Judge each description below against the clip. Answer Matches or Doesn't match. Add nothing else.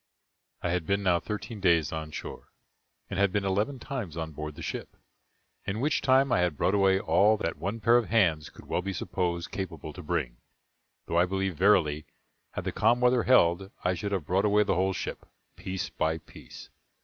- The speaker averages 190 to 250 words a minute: Matches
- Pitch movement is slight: Doesn't match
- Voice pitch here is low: Matches